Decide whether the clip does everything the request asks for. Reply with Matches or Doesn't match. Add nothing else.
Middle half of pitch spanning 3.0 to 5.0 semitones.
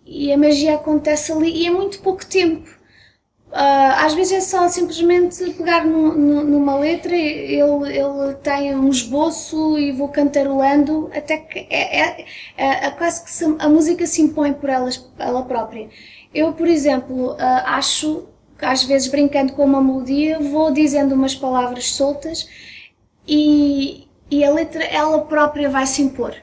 Doesn't match